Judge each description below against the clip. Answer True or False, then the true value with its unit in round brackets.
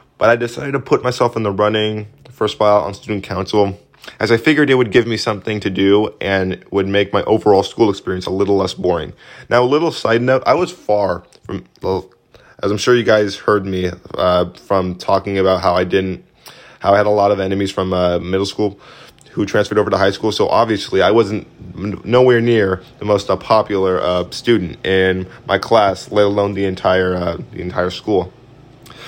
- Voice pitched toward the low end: True (100 Hz)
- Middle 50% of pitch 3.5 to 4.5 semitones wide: False (2.7 semitones)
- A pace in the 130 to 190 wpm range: False (205 wpm)